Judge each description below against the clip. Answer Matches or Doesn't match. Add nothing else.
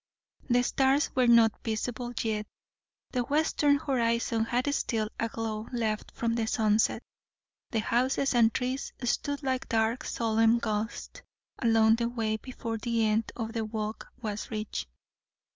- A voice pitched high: Matches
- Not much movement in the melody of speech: Matches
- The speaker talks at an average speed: Matches